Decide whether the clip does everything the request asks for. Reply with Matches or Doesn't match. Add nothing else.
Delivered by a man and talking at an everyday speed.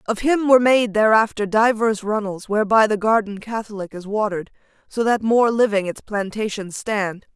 Doesn't match